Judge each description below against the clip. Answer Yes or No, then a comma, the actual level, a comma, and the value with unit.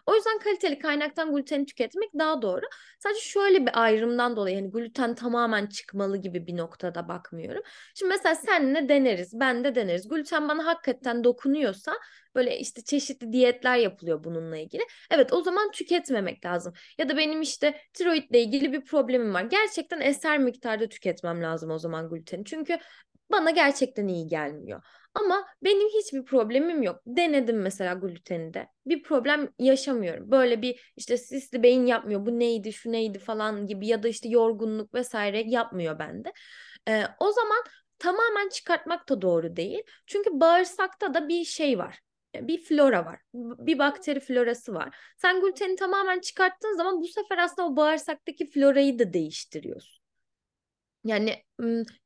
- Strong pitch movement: Yes, wide, 7.3 semitones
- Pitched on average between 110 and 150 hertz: No, very high, 265 Hz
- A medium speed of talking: No, fast, 150 wpm